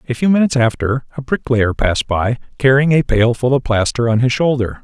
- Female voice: No, male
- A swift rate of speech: Yes, fast, 210 wpm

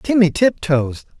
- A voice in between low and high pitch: Yes, medium, 175 Hz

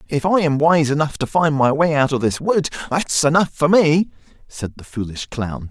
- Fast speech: Yes, fast, 220 wpm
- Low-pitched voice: No, medium, 150 Hz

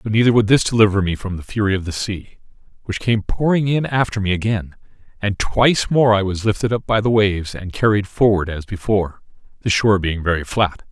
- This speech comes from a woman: No, male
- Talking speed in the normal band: No, fast, 215 wpm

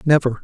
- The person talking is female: No, male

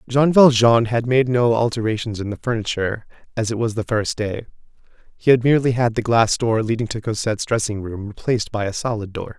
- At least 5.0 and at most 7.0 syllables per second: Yes, 5.9 syllables/s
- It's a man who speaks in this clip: Yes, male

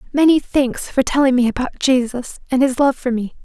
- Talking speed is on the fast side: Yes, fast, 210 wpm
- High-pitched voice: Yes, very high, 260 Hz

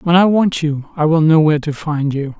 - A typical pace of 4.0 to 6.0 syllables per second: Yes, 5.2 syllables/s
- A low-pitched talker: No, medium, 155 Hz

